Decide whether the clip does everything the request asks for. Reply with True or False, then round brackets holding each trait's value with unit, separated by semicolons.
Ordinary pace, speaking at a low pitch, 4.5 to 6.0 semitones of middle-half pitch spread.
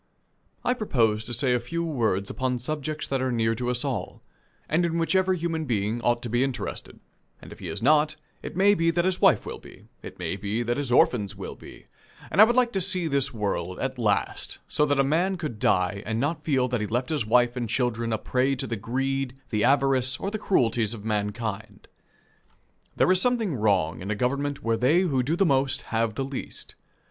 False (220 wpm; 130 Hz; 5.4 semitones)